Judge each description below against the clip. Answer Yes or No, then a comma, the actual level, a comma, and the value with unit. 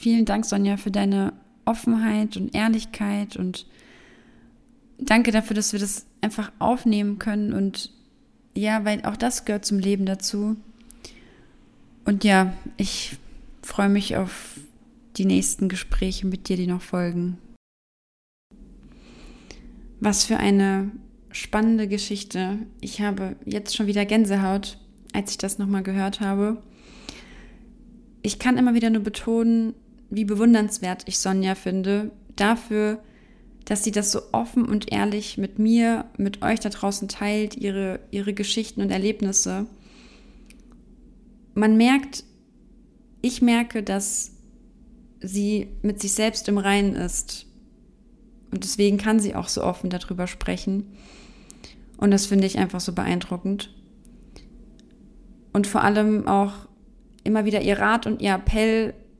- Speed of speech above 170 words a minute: No, average, 130 wpm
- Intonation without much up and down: Yes, narrow, 2.3 semitones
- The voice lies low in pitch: No, high, 215 Hz